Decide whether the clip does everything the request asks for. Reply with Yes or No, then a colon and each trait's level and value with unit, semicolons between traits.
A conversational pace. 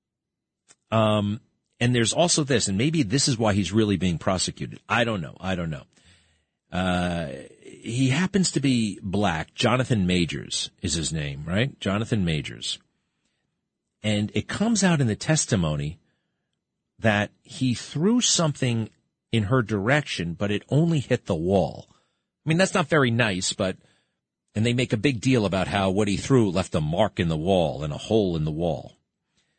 Yes: average, 180 wpm